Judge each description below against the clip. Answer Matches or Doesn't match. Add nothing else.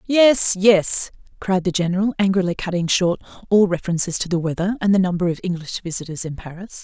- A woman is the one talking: Matches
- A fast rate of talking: Doesn't match